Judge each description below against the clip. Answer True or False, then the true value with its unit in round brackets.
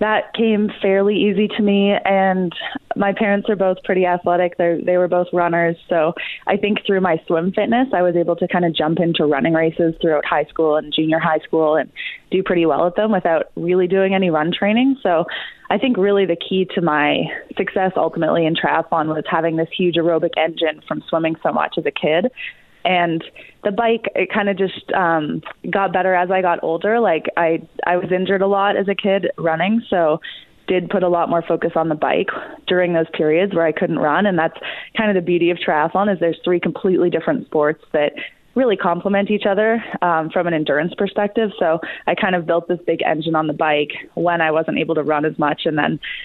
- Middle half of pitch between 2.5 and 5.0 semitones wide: True (3.3 semitones)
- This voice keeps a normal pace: False (215 wpm)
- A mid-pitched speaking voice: True (180 Hz)